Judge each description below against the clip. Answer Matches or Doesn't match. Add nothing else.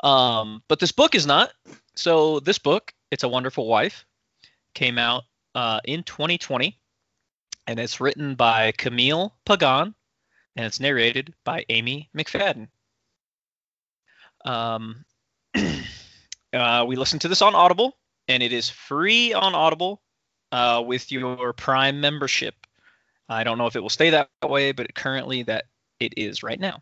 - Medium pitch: Doesn't match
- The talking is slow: Doesn't match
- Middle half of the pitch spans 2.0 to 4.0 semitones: Doesn't match